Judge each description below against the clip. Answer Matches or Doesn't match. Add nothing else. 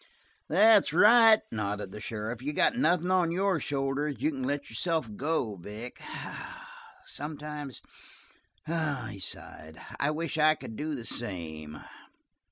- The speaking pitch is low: Doesn't match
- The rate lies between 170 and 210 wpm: Doesn't match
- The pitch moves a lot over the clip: Matches